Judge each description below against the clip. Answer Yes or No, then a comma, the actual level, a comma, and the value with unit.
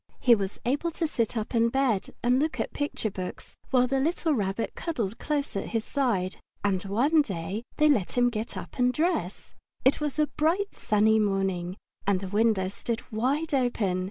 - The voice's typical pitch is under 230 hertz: No, high, 235 Hz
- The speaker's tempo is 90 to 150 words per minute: No, average, 185 wpm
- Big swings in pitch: Yes, wide, 5.9 semitones